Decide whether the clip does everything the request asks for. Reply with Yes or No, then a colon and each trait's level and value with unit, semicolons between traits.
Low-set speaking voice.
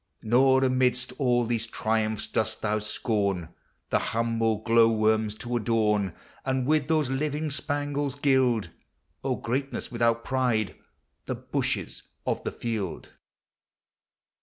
Yes: low, 115 Hz